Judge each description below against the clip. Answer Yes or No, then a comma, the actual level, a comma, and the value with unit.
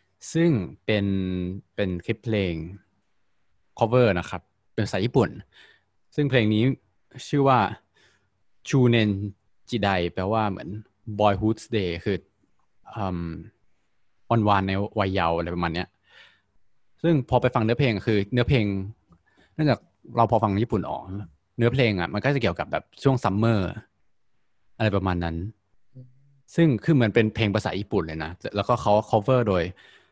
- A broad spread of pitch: No, average, 3.9 semitones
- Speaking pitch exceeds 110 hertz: No, low, 105 Hz